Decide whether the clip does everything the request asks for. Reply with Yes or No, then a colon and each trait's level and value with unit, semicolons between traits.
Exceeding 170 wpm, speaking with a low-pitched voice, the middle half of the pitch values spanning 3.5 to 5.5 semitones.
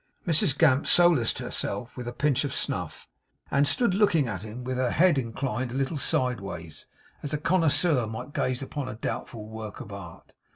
Yes: average, 180 wpm; low, 130 Hz; average, 4.4 semitones